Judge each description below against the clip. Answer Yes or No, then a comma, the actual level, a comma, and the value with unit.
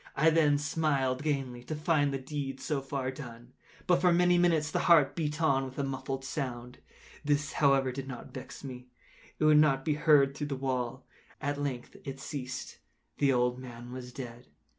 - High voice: No, low, 135 Hz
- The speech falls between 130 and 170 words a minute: No, average, 185 wpm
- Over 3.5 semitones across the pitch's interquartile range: No, narrow, 2.6 semitones